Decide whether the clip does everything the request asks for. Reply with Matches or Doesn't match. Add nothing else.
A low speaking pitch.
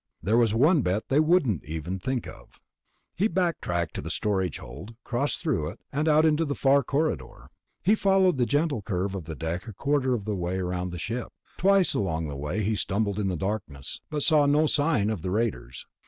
Matches